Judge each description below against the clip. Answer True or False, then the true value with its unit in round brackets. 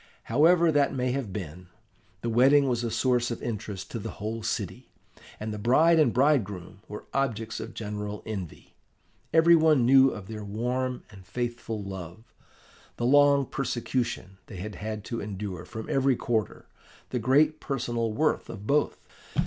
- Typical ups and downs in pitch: True (4.4 semitones)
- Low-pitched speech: True (115 Hz)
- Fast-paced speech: False (160 wpm)